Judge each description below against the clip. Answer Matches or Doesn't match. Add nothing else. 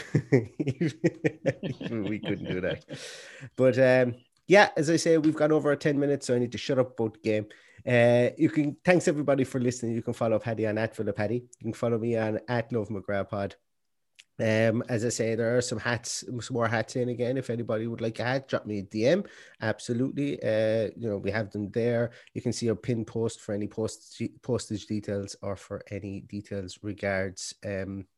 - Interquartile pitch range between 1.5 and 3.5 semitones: Matches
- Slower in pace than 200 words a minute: Doesn't match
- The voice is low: Matches